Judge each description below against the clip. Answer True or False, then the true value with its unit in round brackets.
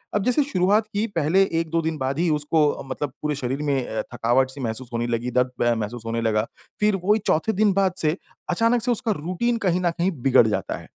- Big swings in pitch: True (7.8 semitones)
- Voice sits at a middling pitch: True (155 Hz)